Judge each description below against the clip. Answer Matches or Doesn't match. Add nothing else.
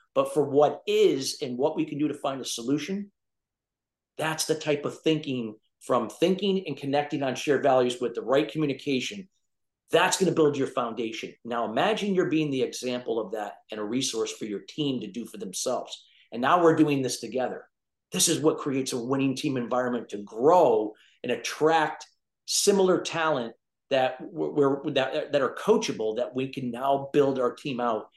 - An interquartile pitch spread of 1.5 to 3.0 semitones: Doesn't match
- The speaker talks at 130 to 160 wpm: Doesn't match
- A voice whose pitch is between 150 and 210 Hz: Doesn't match